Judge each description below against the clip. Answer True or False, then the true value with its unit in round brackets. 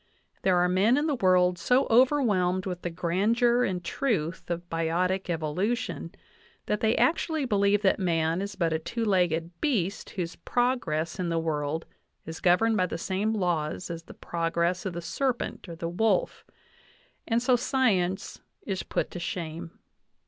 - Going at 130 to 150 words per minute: False (165 wpm)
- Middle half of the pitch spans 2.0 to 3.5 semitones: False (4.7 semitones)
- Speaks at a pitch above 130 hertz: True (185 Hz)